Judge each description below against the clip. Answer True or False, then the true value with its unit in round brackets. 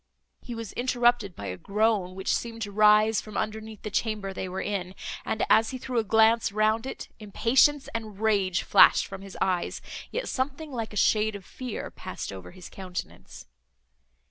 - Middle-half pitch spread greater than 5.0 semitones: False (2.8 semitones)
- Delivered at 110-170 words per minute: False (180 wpm)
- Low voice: False (215 Hz)